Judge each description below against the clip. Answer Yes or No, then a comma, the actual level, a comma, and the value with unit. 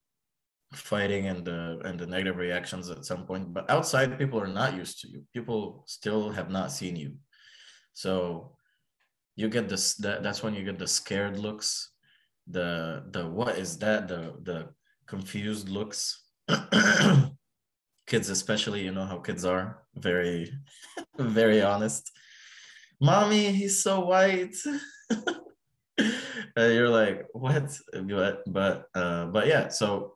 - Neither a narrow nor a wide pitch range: No, wide, 7.8 semitones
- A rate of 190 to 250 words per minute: No, average, 140 wpm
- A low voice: Yes, low, 105 Hz